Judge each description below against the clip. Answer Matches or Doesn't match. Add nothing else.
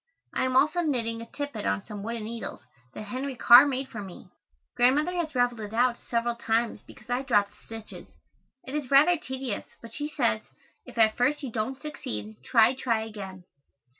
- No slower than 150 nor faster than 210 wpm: Matches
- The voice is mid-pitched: Doesn't match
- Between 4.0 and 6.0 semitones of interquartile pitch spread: Doesn't match